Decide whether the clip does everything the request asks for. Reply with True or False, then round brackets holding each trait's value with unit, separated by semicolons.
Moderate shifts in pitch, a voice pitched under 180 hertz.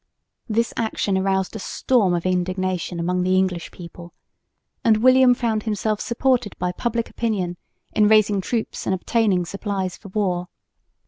False (3.6 semitones; 195 Hz)